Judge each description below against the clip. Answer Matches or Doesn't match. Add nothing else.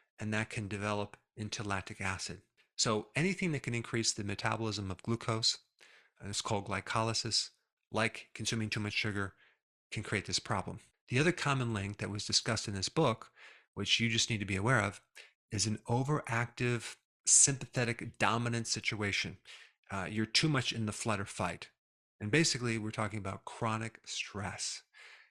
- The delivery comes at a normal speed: Matches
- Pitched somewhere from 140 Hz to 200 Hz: Doesn't match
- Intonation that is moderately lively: Doesn't match